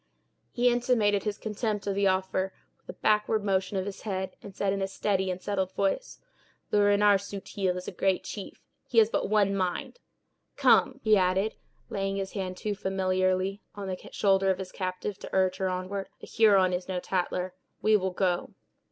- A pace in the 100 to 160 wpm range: No, average, 190 wpm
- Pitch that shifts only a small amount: Yes, narrow, 1.6 semitones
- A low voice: No, high, 195 Hz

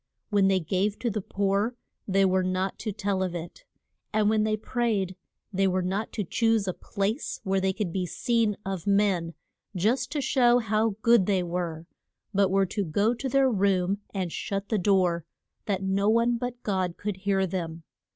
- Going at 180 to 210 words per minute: Yes, average, 190 wpm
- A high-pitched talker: Yes, high, 195 Hz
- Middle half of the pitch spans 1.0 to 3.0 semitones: Yes, narrow, 2.6 semitones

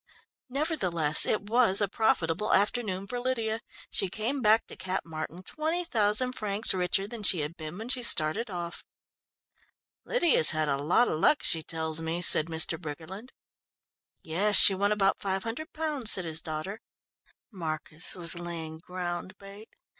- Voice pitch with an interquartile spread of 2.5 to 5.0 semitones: No, wide, 5.4 semitones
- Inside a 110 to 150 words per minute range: No, average, 160 wpm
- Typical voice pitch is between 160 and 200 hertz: Yes, high, 190 Hz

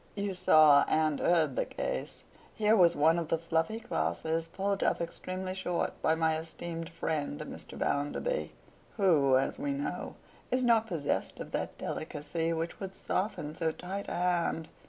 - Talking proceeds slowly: No, average, 155 wpm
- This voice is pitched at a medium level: Yes, medium, 170 Hz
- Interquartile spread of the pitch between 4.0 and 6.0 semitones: No, average, 3.3 semitones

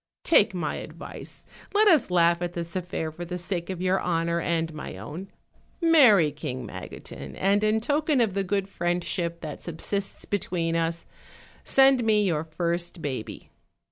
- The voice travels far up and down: No, average, 3.4 semitones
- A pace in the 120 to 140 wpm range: No, average, 160 wpm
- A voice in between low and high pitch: Yes, medium, 175 Hz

